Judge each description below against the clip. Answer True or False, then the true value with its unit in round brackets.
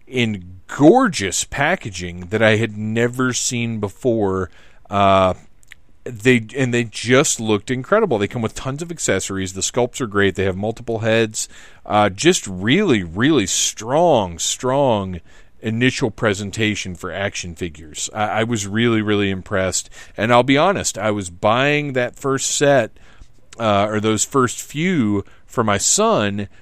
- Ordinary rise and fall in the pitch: True (4.1 semitones)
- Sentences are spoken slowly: False (145 wpm)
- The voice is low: True (110 Hz)